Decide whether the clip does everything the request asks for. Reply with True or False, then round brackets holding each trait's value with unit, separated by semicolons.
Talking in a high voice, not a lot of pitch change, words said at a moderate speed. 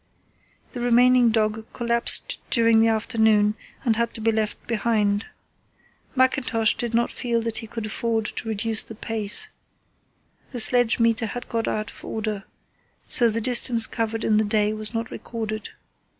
True (225 Hz; 1.4 semitones; 160 wpm)